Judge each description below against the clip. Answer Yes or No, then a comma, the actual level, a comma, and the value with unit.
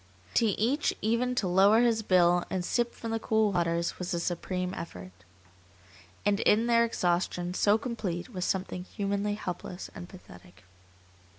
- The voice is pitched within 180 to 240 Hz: Yes, high, 190 Hz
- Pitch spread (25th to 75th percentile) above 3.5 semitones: Yes, average, 4.0 semitones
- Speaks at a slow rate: No, average, 155 wpm